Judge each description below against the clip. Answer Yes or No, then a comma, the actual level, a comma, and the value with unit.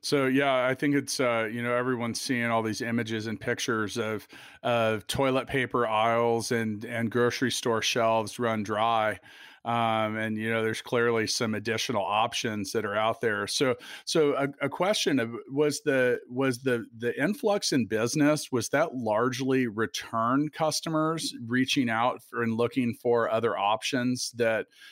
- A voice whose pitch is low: Yes, low, 120 Hz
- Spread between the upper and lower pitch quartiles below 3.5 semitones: Yes, average, 2.7 semitones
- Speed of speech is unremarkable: Yes, average, 165 wpm